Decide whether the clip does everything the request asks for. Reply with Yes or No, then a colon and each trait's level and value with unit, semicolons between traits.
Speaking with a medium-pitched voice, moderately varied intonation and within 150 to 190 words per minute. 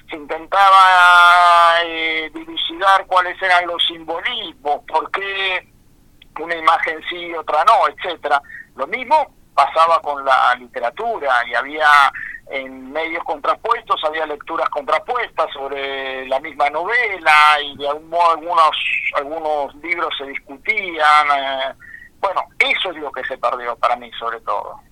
No: medium, 160 Hz; average, 3.7 semitones; average, 130 wpm